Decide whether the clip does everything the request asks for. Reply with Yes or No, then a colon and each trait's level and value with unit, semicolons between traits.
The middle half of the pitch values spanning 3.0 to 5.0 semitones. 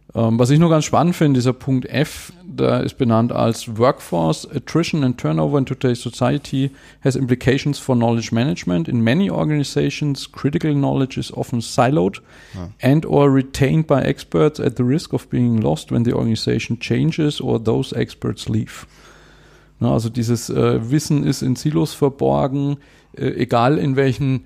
Yes: average, 3.4 semitones